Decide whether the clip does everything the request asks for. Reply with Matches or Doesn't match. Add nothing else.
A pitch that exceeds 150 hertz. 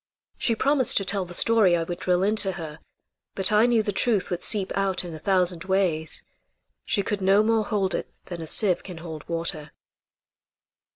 Matches